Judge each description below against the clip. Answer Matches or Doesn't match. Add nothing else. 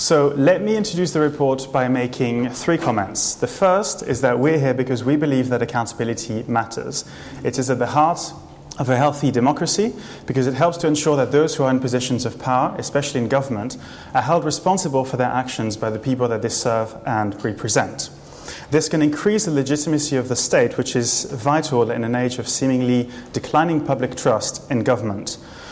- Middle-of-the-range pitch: Doesn't match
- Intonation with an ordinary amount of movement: Matches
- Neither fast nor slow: Matches